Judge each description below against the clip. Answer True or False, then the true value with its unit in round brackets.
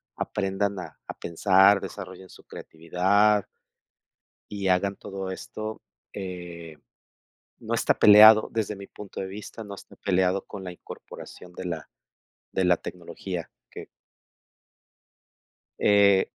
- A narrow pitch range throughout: True (2.1 semitones)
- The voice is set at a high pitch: False (95 Hz)